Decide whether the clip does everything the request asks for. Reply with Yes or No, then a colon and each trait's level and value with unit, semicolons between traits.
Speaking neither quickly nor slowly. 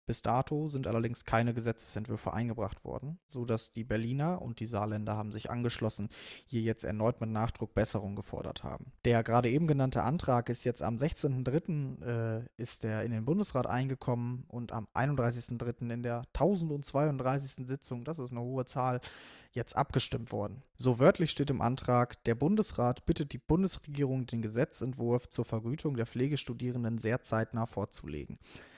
Yes: average, 155 wpm